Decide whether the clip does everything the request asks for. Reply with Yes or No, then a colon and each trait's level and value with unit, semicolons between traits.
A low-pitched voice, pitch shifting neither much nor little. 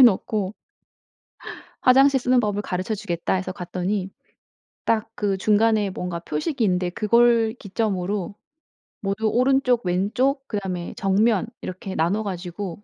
No: high, 205 Hz; average, 3.7 semitones